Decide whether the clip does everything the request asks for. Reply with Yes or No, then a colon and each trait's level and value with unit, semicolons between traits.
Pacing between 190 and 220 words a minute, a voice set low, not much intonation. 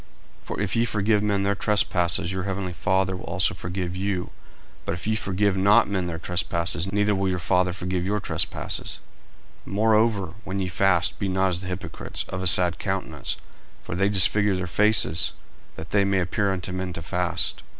Yes: average, 195 wpm; very low, 95 Hz; narrow, 2.1 semitones